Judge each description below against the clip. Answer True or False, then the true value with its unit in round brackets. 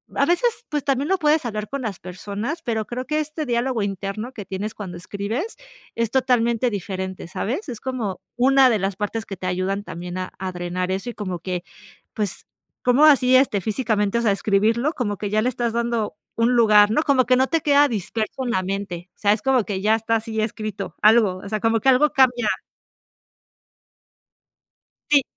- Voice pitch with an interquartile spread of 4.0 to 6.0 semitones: True (4.3 semitones)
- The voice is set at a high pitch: True (225 Hz)